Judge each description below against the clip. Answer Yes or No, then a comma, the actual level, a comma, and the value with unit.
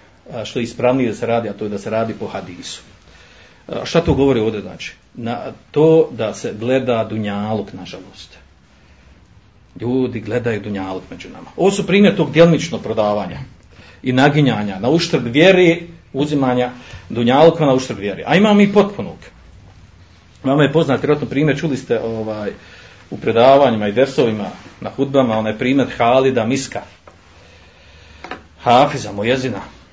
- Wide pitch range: Yes, wide, 6.0 semitones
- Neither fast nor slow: Yes, average, 140 wpm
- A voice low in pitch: Yes, low, 115 Hz